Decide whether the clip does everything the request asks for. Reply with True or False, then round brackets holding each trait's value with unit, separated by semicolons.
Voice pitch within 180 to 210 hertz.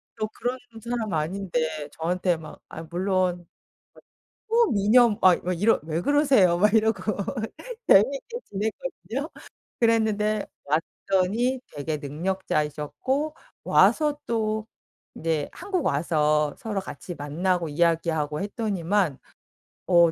True (190 Hz)